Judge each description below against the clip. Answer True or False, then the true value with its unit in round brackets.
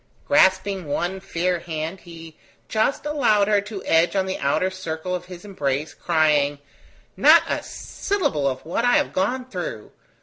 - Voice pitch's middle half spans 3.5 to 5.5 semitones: True (4.3 semitones)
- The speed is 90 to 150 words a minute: False (160 wpm)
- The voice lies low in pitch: False (185 Hz)